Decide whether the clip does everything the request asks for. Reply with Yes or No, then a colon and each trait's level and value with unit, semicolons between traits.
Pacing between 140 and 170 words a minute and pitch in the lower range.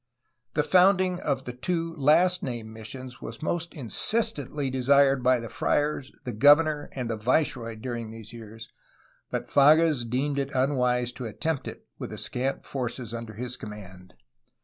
Yes: average, 155 wpm; low, 130 Hz